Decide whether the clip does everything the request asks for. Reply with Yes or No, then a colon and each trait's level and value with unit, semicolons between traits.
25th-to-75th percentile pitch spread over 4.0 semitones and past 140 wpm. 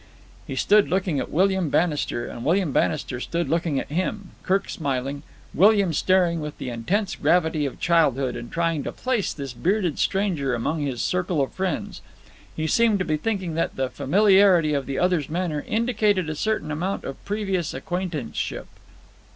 Yes: average, 4.8 semitones; average, 165 wpm